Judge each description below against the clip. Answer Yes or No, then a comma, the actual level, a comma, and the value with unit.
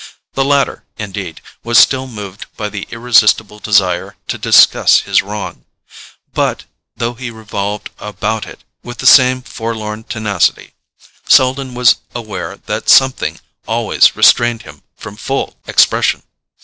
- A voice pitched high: No, low, 110 Hz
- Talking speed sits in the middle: No, slow, 130 wpm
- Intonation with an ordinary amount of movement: Yes, average, 3.0 semitones